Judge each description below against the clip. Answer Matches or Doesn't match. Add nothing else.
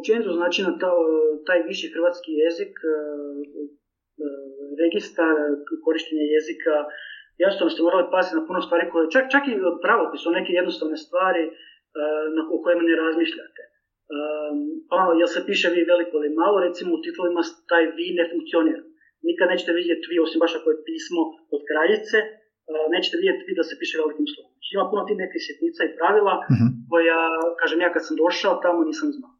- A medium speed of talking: Doesn't match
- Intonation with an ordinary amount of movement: Matches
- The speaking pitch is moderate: Matches